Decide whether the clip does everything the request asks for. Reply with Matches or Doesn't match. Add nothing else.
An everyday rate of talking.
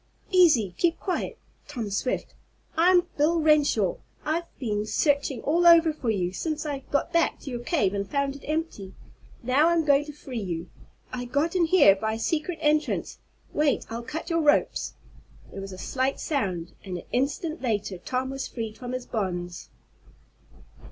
Matches